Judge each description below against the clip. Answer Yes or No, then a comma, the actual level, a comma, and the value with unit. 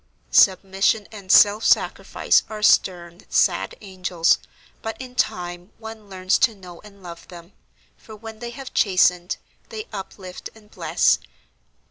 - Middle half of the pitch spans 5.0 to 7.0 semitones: No, average, 3.3 semitones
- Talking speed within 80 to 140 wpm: Yes, slow, 135 wpm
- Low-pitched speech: No, high, 195 Hz